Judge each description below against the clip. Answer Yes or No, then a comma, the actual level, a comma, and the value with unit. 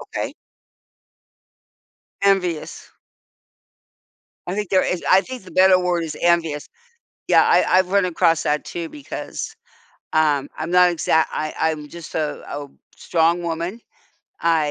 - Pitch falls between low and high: Yes, medium, 170 Hz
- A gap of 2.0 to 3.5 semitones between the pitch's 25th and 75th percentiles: Yes, narrow, 2.6 semitones